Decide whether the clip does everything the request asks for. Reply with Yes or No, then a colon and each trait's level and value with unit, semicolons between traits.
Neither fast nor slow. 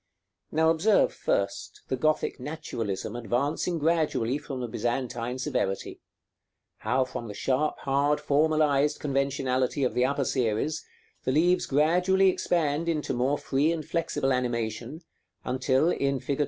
No: slow, 130 wpm